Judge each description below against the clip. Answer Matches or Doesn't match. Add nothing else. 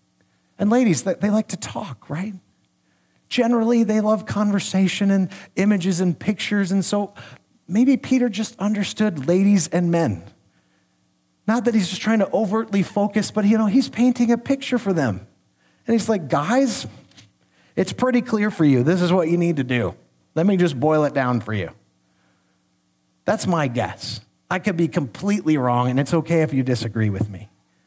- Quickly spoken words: Doesn't match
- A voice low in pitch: Doesn't match